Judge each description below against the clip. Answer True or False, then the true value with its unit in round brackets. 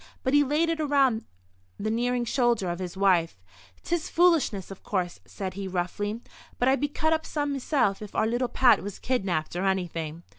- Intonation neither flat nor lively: False (6.7 semitones)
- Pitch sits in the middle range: False (225 Hz)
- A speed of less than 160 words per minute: False (190 wpm)